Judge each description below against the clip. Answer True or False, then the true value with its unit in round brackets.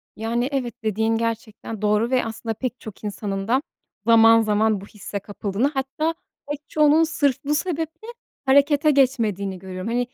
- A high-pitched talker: True (230 Hz)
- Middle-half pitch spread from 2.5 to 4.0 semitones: False (4.7 semitones)